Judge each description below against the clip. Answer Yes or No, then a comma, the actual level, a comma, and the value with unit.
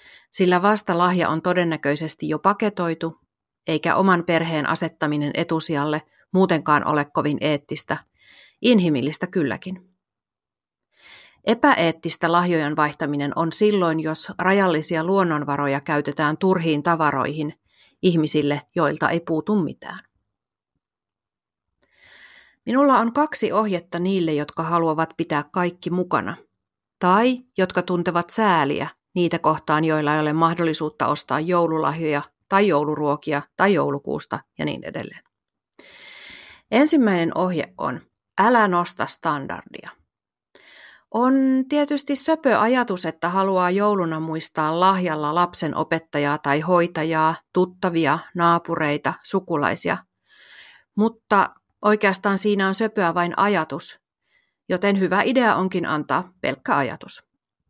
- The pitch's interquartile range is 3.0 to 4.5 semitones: Yes, average, 3.8 semitones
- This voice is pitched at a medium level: Yes, medium, 170 Hz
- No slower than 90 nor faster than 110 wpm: Yes, average, 105 wpm